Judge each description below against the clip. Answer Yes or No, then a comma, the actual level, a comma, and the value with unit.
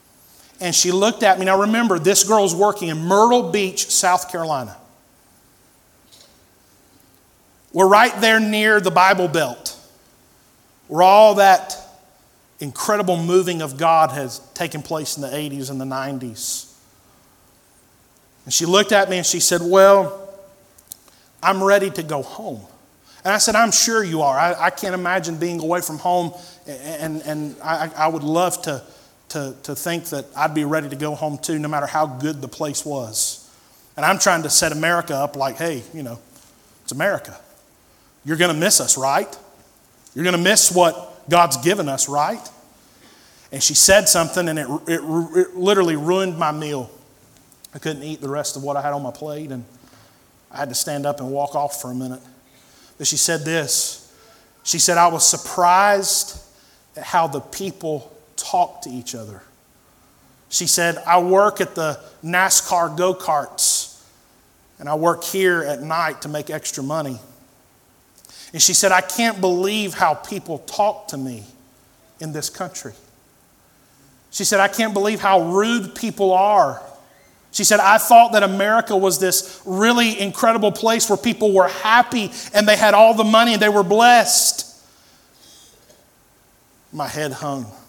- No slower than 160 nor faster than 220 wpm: Yes, average, 165 wpm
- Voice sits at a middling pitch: Yes, medium, 170 Hz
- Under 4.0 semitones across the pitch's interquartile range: No, average, 5.1 semitones